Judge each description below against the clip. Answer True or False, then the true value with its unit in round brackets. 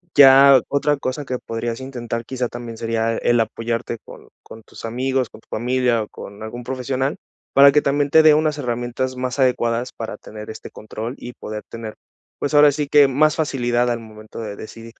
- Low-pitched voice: True (125 Hz)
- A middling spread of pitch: True (3.1 semitones)